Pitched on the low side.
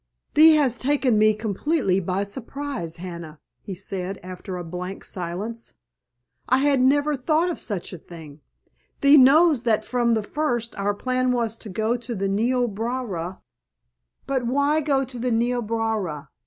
No: high, 230 Hz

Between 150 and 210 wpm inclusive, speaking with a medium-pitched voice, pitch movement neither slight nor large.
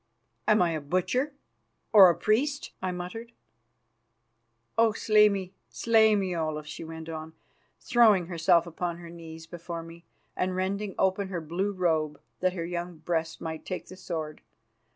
Yes: average, 155 wpm; medium, 180 Hz; average, 3.4 semitones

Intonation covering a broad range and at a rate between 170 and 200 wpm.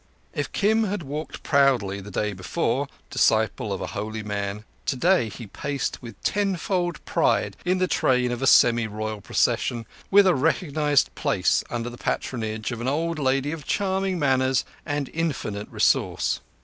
No: wide, 6.9 semitones; average, 160 wpm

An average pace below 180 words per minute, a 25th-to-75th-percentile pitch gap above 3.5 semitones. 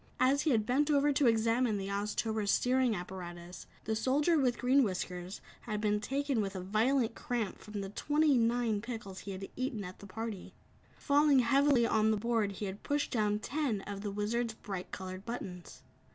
No: average, 185 wpm; average, 4.3 semitones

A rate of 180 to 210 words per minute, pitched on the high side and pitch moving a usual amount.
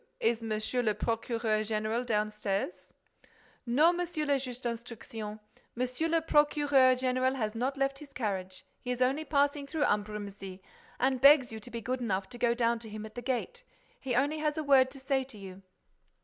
Yes: average, 185 wpm; high, 245 Hz; average, 4.3 semitones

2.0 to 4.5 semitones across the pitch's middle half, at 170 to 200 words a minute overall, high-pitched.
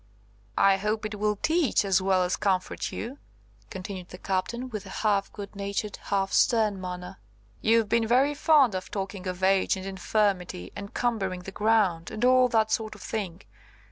Yes: average, 2.9 semitones; average, 175 wpm; high, 200 Hz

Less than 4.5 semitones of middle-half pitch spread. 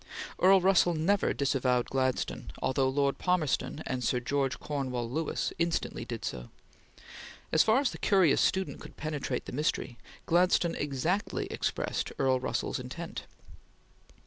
No: average, 5.1 semitones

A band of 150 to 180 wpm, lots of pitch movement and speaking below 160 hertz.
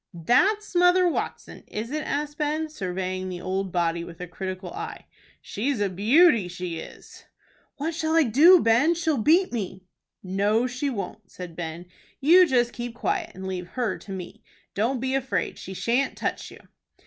No: average, 170 wpm; wide, 8.3 semitones; high, 230 Hz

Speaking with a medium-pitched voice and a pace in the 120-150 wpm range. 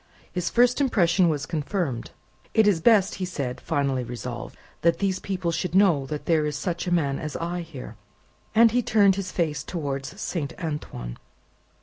No: medium, 170 Hz; average, 165 wpm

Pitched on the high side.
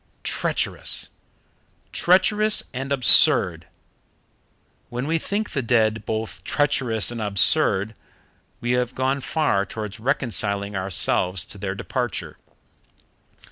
No: low, 120 Hz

